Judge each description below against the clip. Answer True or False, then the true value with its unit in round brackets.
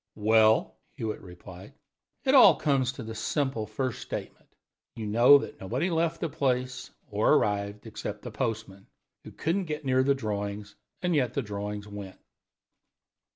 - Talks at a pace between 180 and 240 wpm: False (155 wpm)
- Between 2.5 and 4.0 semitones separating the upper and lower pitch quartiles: False (4.7 semitones)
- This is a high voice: False (110 Hz)